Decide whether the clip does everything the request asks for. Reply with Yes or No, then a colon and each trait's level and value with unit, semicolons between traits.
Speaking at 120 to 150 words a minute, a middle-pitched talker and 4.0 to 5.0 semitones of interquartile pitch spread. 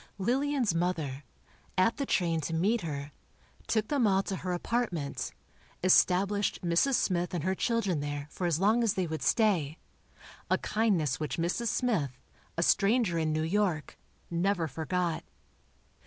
Yes: average, 145 wpm; medium, 180 Hz; average, 4.7 semitones